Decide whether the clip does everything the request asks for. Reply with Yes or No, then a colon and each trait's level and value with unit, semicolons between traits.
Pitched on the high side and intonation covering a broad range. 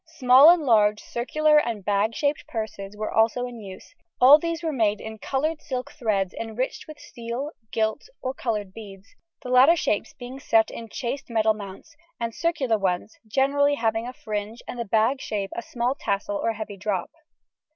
No: high, 230 Hz; average, 4.1 semitones